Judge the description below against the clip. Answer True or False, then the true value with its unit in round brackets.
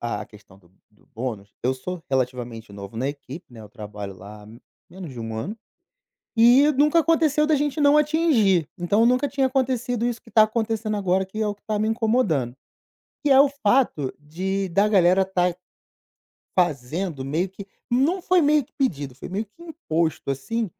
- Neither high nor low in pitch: False (195 Hz)